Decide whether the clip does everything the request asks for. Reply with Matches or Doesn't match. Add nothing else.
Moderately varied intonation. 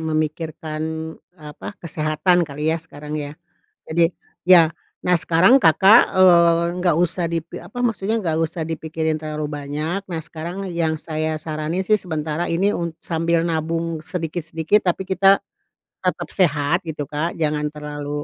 Doesn't match